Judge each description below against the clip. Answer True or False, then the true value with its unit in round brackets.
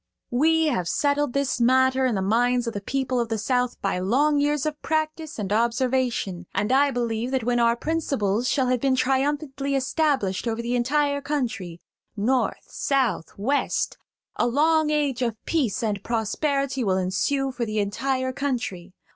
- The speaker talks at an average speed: True (160 wpm)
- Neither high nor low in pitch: False (255 Hz)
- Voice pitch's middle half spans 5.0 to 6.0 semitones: False (3.8 semitones)